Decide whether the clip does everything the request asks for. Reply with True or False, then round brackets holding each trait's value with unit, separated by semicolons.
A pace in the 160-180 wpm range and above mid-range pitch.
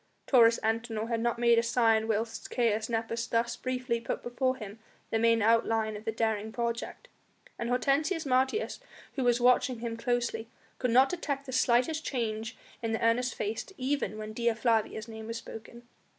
True (175 wpm; 230 Hz)